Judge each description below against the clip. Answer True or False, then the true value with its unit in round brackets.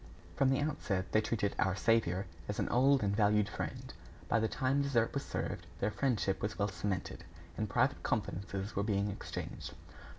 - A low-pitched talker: True (105 Hz)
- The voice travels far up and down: False (3.4 semitones)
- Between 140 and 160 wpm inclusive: False (175 wpm)